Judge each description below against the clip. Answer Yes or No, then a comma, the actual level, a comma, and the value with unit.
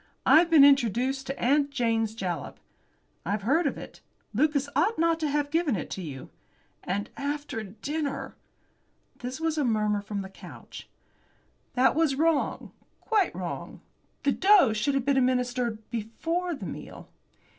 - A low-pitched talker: No, very high, 270 Hz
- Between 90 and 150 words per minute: Yes, average, 145 wpm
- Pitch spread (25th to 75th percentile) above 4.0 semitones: Yes, wide, 5.5 semitones